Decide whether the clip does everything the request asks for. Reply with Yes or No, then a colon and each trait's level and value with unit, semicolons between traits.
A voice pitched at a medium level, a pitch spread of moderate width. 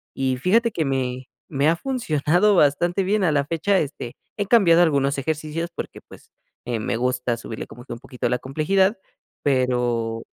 No: medium, 145 Hz; wide, 5.7 semitones